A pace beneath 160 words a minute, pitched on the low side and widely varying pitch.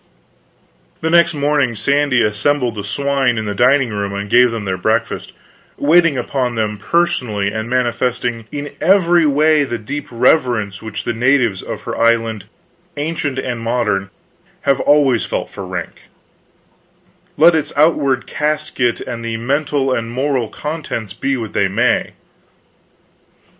No: average, 140 wpm; low, 125 Hz; average, 4.6 semitones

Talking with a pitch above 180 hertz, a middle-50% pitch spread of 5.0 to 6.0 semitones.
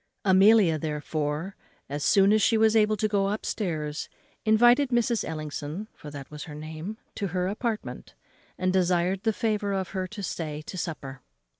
Yes: high, 190 Hz; wide, 5.6 semitones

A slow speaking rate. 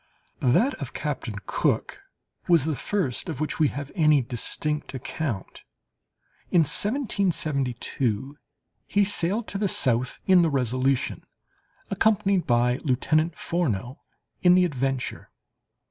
Yes: slow, 115 wpm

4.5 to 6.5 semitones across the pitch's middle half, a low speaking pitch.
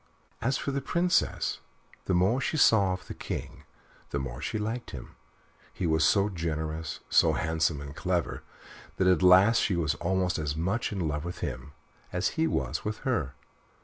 Yes: average, 5.2 semitones; very low, 90 Hz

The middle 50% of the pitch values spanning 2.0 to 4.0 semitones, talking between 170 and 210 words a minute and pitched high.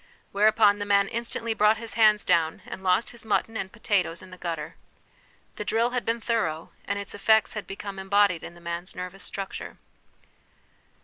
Yes: average, 3.3 semitones; average, 185 wpm; high, 200 Hz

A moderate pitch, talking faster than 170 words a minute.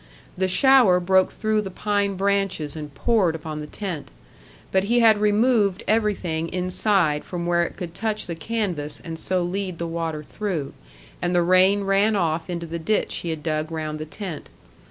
Yes: medium, 180 Hz; average, 180 wpm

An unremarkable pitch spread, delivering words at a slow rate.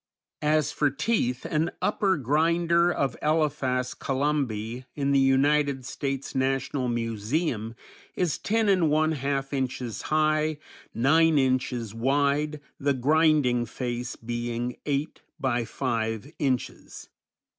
Yes: average, 3.7 semitones; slow, 115 wpm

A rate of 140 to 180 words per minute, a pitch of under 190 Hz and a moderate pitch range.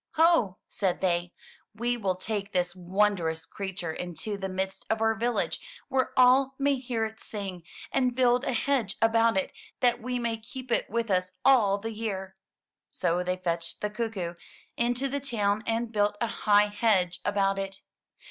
No: average, 170 wpm; high, 210 Hz; average, 3.9 semitones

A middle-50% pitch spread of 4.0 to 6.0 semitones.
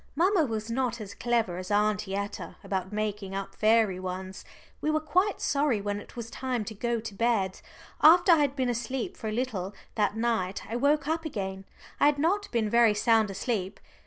Yes: average, 4.6 semitones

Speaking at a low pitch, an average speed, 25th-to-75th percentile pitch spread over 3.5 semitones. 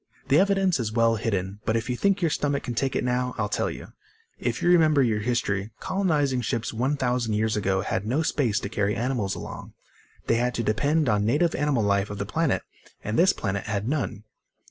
No: low, 120 Hz; fast, 210 wpm; average, 5.2 semitones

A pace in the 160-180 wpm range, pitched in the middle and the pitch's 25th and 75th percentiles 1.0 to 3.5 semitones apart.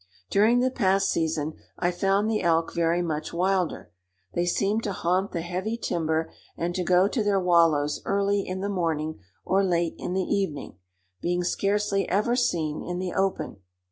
Yes: average, 170 wpm; medium, 180 Hz; average, 2.9 semitones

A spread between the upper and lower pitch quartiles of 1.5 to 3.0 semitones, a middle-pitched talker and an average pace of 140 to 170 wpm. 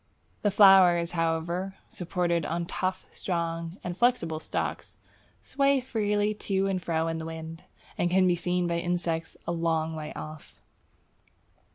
Yes: narrow, 2.6 semitones; medium, 175 Hz; average, 145 wpm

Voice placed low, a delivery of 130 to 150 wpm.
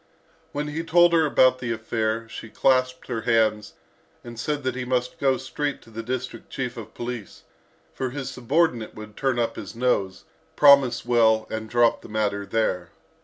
No: low, 120 Hz; average, 175 wpm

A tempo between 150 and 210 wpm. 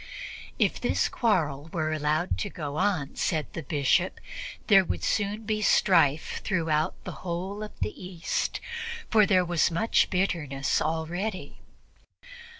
No: slow, 135 wpm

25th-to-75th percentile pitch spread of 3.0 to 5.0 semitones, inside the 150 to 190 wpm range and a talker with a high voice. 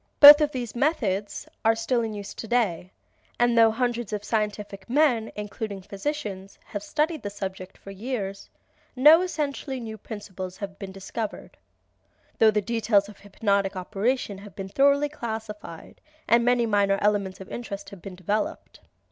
Yes: average, 3.5 semitones; average, 155 wpm; high, 210 Hz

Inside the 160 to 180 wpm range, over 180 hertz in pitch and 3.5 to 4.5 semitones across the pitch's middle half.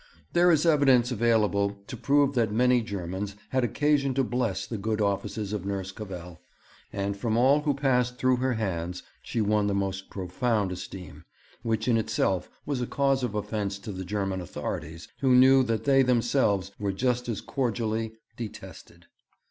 No: average, 170 wpm; low, 110 Hz; average, 4.2 semitones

